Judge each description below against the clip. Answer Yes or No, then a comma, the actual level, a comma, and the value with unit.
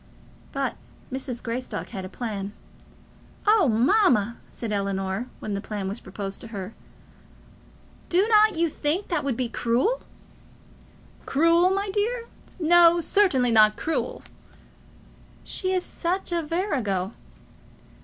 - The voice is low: No, very high, 260 Hz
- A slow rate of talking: Yes, slow, 125 wpm